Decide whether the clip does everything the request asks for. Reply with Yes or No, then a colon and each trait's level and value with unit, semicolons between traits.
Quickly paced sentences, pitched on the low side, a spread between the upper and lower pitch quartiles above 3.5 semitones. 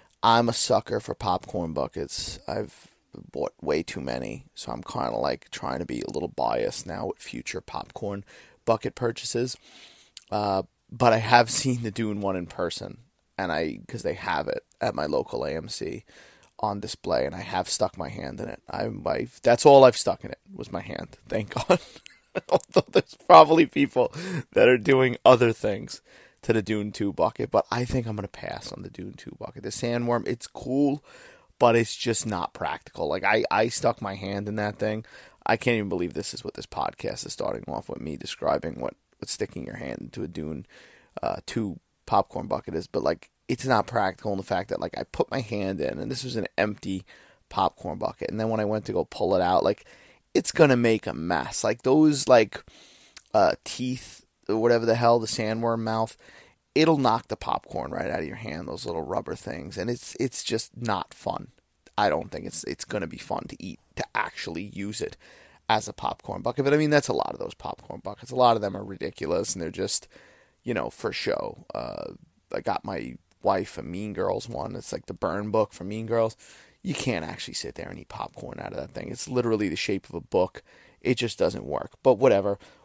No: fast, 215 wpm; low, 115 Hz; average, 3.2 semitones